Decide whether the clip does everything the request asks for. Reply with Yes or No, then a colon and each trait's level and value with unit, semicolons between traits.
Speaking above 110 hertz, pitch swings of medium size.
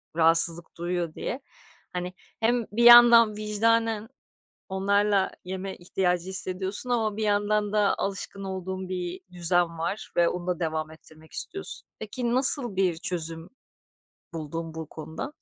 Yes: high, 190 Hz; average, 3.7 semitones